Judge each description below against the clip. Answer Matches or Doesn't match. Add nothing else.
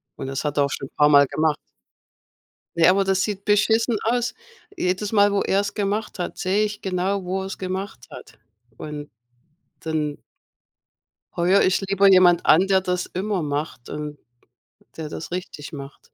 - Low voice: Doesn't match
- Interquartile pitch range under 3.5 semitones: Doesn't match